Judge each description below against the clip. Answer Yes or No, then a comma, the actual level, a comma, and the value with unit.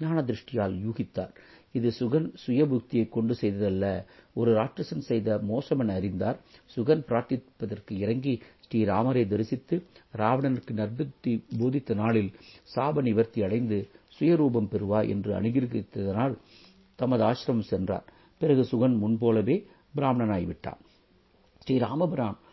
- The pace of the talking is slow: No, average, 85 wpm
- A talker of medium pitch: No, low, 115 Hz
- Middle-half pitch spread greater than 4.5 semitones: No, average, 3.5 semitones